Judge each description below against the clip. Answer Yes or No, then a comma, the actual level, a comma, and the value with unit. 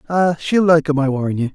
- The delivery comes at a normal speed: No, fast, 270 wpm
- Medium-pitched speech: Yes, medium, 155 Hz